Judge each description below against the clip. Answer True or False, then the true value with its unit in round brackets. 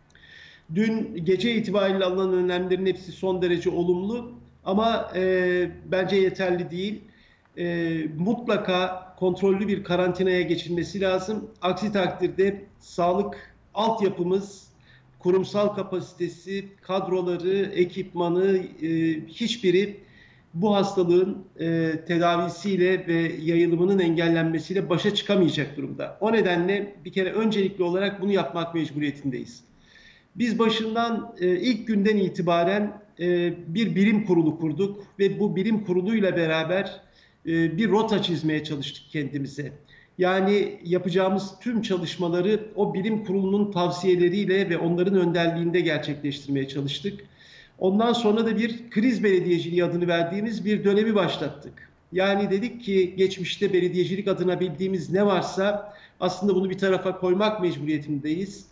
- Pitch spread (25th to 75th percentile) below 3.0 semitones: True (2.5 semitones)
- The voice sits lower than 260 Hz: True (185 Hz)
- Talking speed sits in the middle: True (110 wpm)